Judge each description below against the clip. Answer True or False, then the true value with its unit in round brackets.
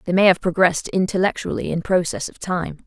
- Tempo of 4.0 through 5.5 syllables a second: False (5.9 syllables/s)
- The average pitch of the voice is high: False (180 Hz)